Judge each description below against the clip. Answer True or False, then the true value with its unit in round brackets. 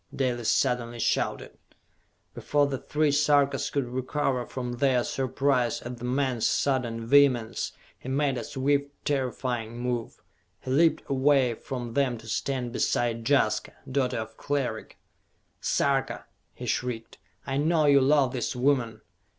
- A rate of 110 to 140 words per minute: True (135 wpm)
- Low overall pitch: True (130 Hz)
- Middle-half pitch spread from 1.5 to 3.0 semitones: True (2.6 semitones)